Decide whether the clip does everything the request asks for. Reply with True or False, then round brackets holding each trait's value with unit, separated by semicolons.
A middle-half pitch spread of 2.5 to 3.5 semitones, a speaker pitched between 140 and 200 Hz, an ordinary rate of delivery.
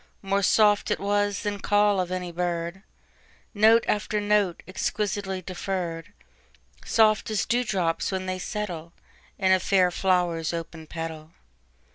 False (3.0 semitones; 190 Hz; 120 wpm)